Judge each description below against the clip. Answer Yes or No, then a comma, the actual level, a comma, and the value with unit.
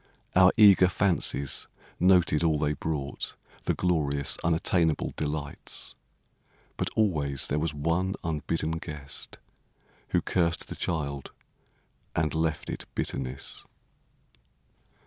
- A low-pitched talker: Yes, very low, 80 Hz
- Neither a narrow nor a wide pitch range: Yes, average, 3.2 semitones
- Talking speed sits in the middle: No, slow, 105 wpm